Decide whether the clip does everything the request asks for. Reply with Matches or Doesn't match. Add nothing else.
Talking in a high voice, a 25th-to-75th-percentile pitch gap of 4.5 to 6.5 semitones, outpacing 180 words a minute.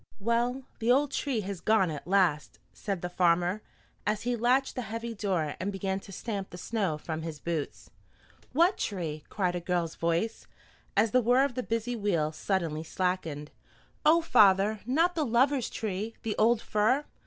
Doesn't match